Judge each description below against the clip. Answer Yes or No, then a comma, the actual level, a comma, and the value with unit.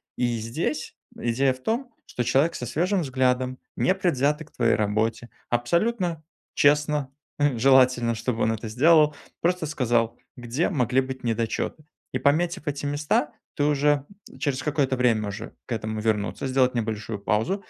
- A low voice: Yes, low, 130 Hz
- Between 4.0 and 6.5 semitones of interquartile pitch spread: Yes, average, 4.3 semitones